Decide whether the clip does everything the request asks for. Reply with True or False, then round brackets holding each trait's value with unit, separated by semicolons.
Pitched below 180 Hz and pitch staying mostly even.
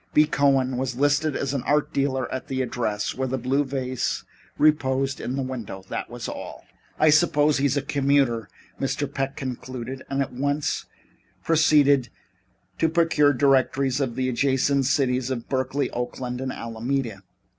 True (135 Hz; 1.9 semitones)